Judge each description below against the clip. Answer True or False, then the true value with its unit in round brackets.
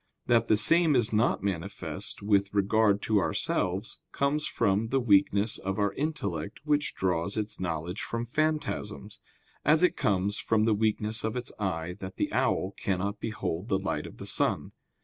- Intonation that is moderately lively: True (3.2 semitones)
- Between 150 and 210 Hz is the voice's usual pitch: False (105 Hz)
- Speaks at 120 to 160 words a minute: False (170 wpm)